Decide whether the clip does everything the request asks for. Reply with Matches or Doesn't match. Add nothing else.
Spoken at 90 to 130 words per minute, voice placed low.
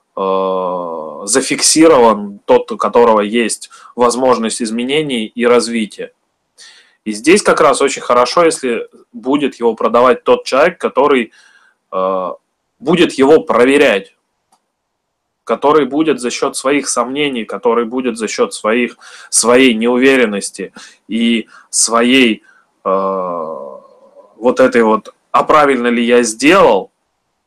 Matches